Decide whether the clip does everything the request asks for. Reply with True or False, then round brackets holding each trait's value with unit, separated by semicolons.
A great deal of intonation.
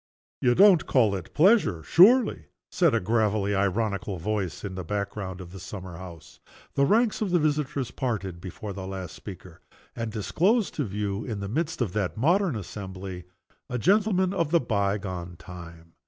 True (8.0 semitones)